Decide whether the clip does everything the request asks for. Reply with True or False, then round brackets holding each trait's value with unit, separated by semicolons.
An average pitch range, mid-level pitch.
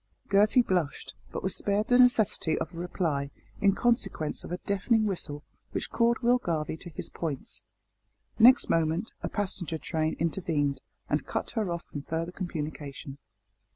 True (4.8 semitones; 175 Hz)